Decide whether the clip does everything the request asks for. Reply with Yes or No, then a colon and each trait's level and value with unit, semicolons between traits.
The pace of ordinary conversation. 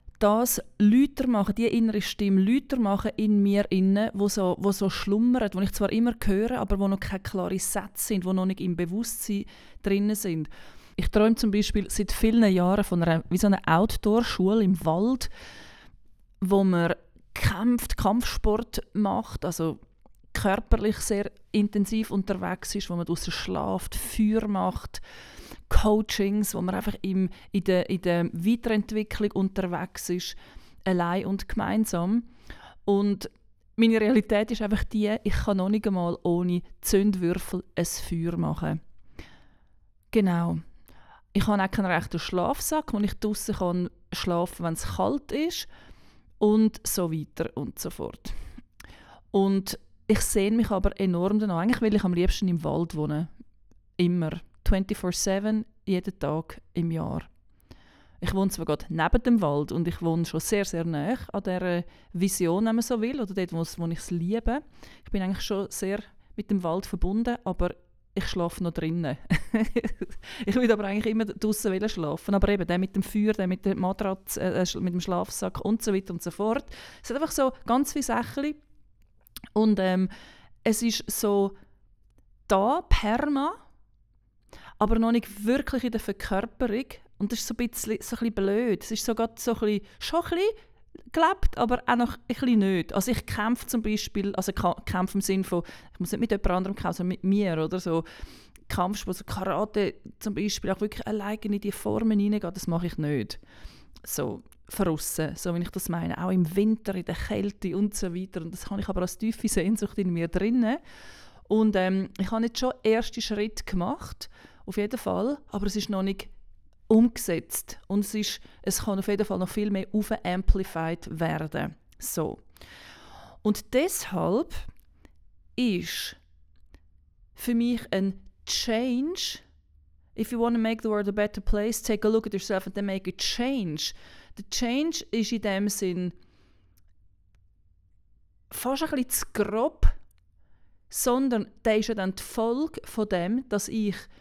Yes: average, 165 wpm